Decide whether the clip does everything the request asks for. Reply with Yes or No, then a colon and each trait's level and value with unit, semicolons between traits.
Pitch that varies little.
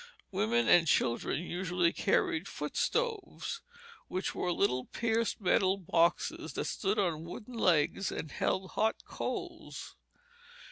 No: average, 4.2 semitones